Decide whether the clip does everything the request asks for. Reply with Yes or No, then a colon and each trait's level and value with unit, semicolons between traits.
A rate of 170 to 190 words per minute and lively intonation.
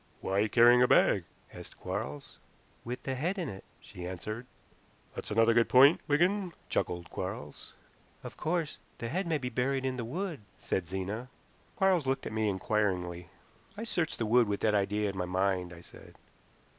Yes: average, 175 wpm; wide, 6.4 semitones